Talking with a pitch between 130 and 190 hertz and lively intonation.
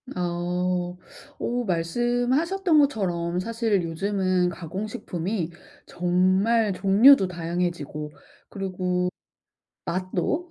No: medium, 185 Hz; average, 4.1 semitones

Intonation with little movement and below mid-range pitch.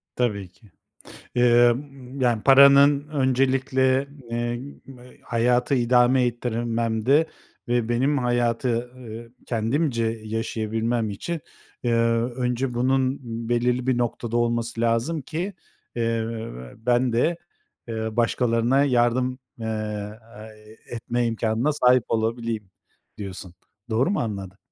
Yes: narrow, 2.2 semitones; low, 120 Hz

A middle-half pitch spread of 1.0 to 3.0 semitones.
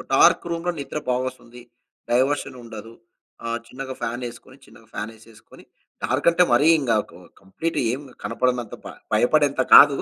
No: average, 3.6 semitones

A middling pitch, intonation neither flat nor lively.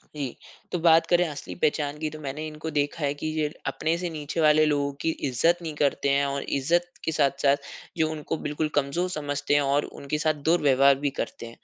No: medium, 150 Hz; narrow, 2.2 semitones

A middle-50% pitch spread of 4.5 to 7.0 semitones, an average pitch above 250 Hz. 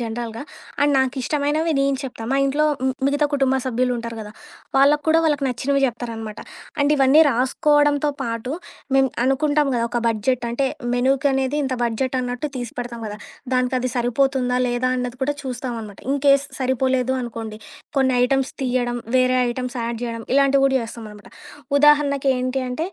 No: narrow, 2.4 semitones; very high, 260 Hz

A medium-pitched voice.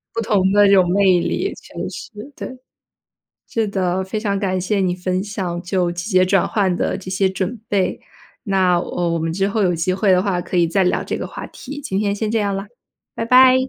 No: high, 195 Hz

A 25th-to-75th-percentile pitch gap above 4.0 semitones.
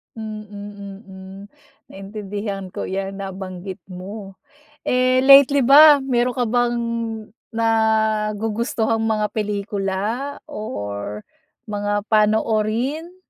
No: average, 3.2 semitones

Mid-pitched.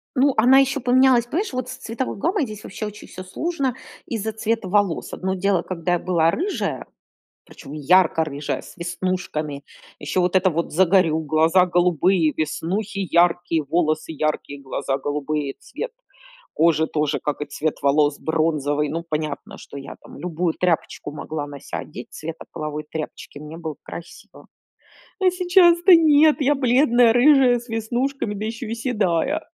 Yes: medium, 180 Hz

